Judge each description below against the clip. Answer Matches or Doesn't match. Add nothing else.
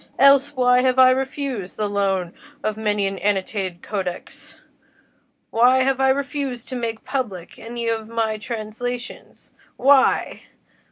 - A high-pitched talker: Matches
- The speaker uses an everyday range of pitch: Matches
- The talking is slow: Matches